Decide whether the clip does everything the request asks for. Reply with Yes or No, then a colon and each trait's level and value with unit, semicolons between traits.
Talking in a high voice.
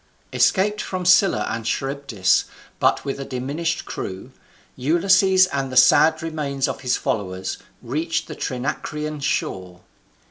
No: medium, 140 Hz